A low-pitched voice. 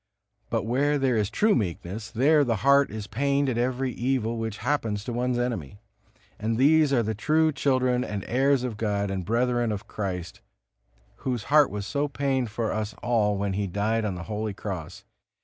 Yes: low, 115 Hz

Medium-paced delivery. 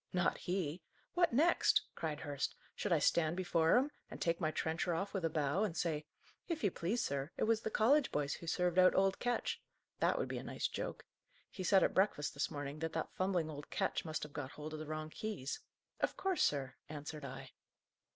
No: fast, 215 wpm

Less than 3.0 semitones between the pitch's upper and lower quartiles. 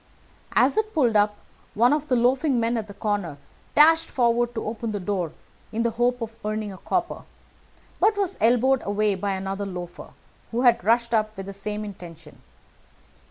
No: average, 3.3 semitones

